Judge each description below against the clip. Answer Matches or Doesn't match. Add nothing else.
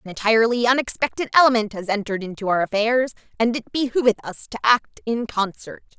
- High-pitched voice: Matches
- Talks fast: Doesn't match